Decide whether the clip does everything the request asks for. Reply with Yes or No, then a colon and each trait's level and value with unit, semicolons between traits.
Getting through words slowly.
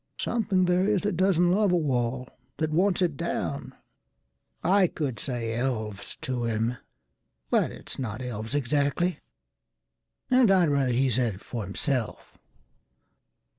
Yes: slow, 125 wpm